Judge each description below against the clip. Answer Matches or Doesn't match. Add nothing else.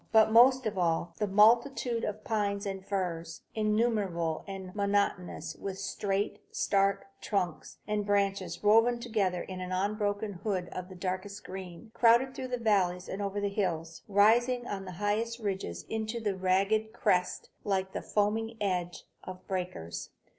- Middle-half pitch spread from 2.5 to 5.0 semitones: Matches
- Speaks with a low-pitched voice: Doesn't match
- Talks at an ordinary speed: Matches